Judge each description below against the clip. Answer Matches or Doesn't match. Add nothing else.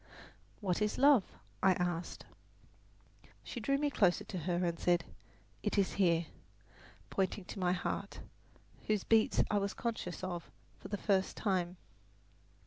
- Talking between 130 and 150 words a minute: Matches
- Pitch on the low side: Doesn't match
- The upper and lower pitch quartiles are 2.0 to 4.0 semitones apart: Matches